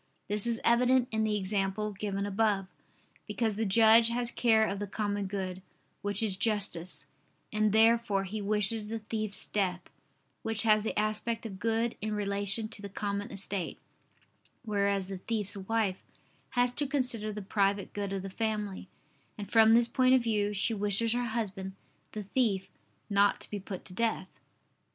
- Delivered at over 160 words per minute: Yes, average, 170 wpm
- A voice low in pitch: No, high, 210 Hz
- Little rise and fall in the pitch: Yes, narrow, 2.2 semitones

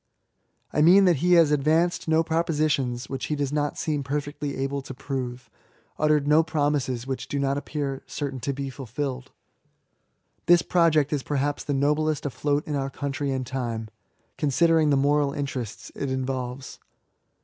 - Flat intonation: Yes, narrow, 2.2 semitones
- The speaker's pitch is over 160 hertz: No, medium, 145 Hz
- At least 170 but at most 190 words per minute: No, average, 160 wpm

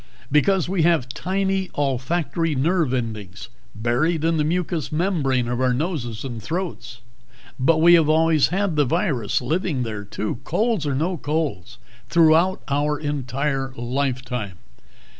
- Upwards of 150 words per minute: No, average, 140 wpm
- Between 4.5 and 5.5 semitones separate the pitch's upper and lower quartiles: Yes, average, 5.2 semitones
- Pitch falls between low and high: Yes, medium, 150 Hz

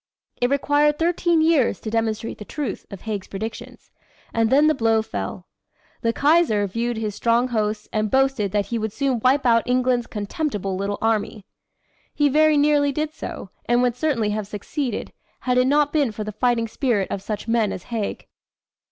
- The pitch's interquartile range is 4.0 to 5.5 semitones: Yes, average, 4.8 semitones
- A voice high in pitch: Yes, high, 230 Hz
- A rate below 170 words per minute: No, average, 180 wpm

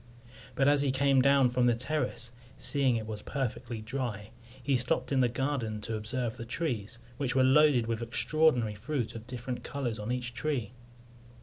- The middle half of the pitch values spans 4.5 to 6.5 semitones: No, average, 3.2 semitones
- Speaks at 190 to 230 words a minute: No, average, 180 wpm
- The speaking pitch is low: Yes, low, 125 Hz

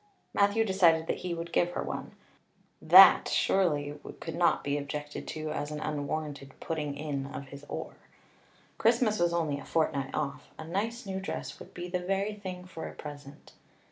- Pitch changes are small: No, average, 4.0 semitones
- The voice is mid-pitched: Yes, medium, 160 Hz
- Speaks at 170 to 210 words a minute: Yes, average, 175 wpm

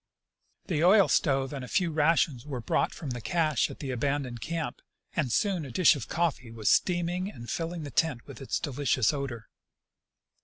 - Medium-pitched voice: Yes, medium, 145 Hz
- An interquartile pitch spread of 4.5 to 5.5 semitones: Yes, average, 4.8 semitones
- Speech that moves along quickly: No, average, 185 wpm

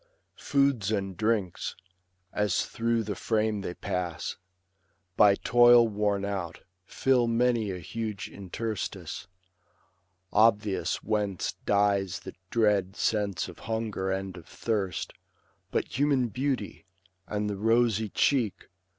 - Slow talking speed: Yes, slow, 115 wpm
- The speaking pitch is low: Yes, low, 105 Hz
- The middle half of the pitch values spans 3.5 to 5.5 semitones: No, average, 2.9 semitones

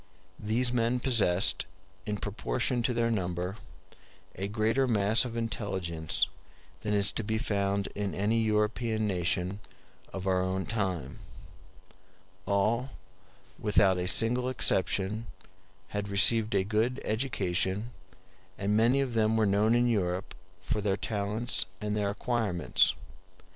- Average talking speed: No, slow, 125 wpm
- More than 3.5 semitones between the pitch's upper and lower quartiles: No, average, 3.0 semitones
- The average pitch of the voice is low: Yes, low, 105 Hz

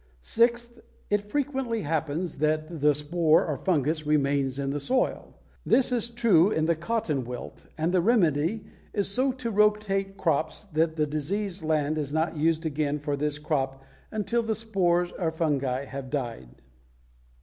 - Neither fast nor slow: Yes, average, 160 wpm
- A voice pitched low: No, medium, 160 Hz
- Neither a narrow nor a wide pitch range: No, wide, 6.0 semitones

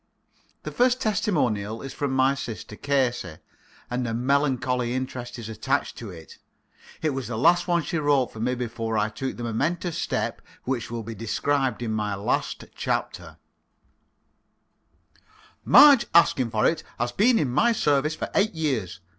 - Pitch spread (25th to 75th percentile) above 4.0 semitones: Yes, average, 4.7 semitones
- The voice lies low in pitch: Yes, low, 130 Hz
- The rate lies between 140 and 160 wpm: Yes, average, 155 wpm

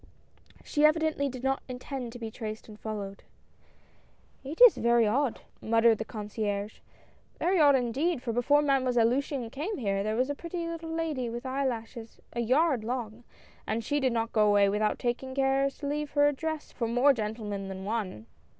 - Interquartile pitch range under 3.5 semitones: No, average, 4.3 semitones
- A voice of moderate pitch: No, high, 245 Hz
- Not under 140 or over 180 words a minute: Yes, average, 175 wpm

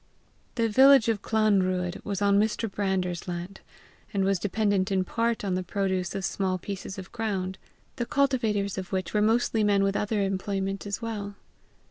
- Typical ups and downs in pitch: No, narrow, 2.3 semitones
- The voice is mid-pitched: No, high, 200 Hz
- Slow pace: No, average, 175 wpm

